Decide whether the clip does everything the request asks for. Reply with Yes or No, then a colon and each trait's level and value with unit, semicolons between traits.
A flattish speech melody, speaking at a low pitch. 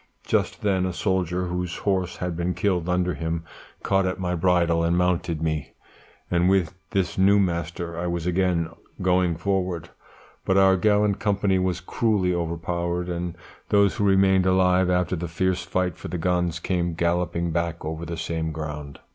Yes: narrow, 1.7 semitones; very low, 90 Hz